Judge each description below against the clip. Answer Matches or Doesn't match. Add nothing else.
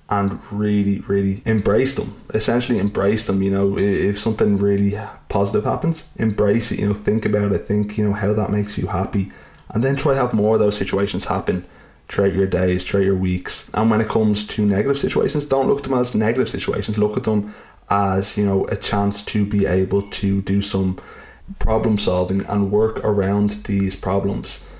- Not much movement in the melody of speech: Matches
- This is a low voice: Matches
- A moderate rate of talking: Matches